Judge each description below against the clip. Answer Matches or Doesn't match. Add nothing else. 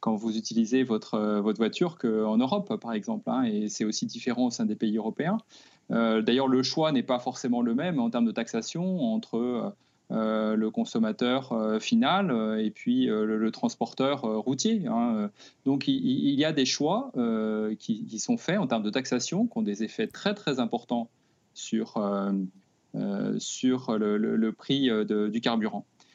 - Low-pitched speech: Matches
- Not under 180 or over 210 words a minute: Matches